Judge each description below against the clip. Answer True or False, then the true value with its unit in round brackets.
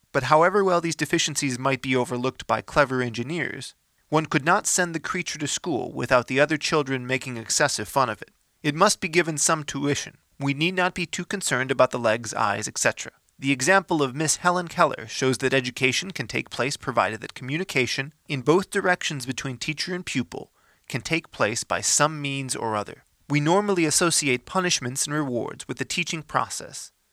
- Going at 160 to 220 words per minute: True (190 wpm)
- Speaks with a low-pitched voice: False (150 Hz)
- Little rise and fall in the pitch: False (4.8 semitones)